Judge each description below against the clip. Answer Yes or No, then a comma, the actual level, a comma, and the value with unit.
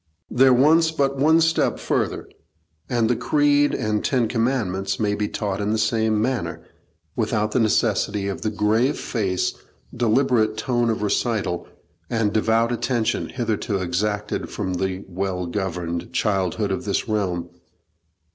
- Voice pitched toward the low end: Yes, low, 110 Hz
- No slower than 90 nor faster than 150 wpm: Yes, average, 140 wpm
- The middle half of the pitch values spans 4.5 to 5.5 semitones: No, average, 3.6 semitones